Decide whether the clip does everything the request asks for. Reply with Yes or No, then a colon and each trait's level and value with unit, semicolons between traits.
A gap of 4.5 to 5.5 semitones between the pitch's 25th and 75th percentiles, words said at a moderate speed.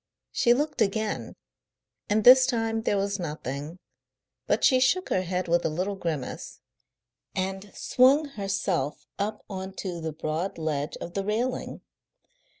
Yes: average, 4.9 semitones; average, 145 wpm